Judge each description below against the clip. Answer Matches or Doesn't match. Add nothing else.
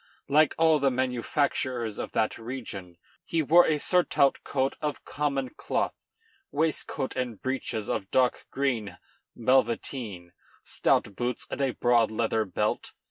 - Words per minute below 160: Matches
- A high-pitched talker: Doesn't match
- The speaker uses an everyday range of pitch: Matches